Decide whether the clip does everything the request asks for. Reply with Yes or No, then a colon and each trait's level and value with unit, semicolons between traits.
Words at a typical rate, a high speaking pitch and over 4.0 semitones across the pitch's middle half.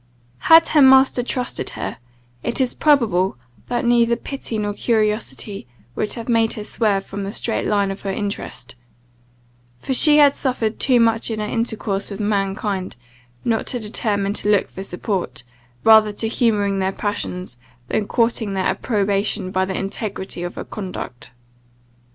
No: average, 155 wpm; high, 210 Hz; average, 3.1 semitones